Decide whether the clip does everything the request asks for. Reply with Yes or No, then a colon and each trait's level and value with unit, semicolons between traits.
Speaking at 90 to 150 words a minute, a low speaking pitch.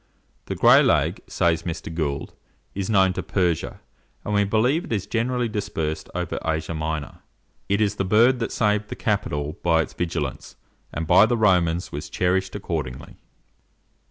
No: average, 160 wpm; very low, 90 Hz